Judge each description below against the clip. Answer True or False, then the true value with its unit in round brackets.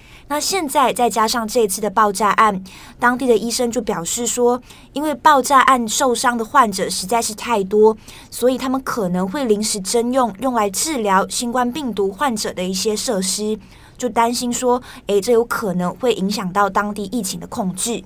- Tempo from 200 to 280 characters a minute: True (275 characters per minute)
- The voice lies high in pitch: True (230 Hz)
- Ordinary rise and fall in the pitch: True (3.2 semitones)